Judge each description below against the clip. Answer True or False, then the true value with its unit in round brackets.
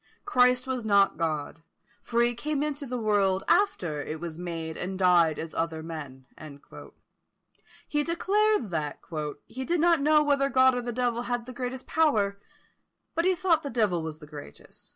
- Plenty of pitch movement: True (9.0 semitones)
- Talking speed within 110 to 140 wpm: False (175 wpm)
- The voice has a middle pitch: False (235 Hz)